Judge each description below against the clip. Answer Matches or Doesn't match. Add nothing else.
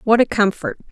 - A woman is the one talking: Matches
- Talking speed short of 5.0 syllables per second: Doesn't match